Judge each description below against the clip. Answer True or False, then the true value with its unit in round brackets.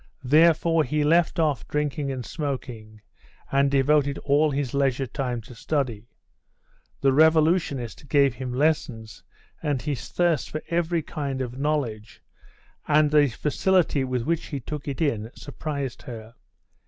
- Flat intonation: False (3.2 semitones)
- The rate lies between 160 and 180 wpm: False (140 wpm)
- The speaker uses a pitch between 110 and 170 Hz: True (140 Hz)